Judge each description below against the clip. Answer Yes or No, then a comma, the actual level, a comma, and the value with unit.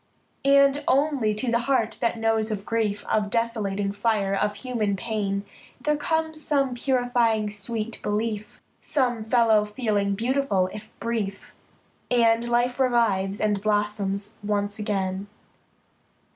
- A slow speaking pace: Yes, slow, 125 wpm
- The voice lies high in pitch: Yes, high, 220 Hz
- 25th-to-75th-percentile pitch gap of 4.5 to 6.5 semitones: No, average, 2.9 semitones